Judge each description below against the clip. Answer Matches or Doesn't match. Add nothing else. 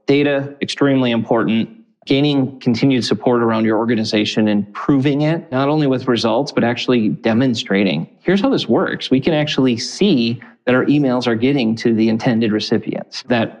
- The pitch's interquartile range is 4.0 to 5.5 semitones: Doesn't match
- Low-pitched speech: Matches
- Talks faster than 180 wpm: Doesn't match